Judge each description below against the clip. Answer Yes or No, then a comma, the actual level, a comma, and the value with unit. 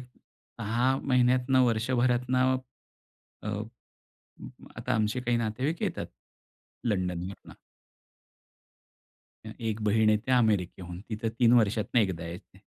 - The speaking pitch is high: No, low, 115 Hz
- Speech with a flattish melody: No, average, 3.2 semitones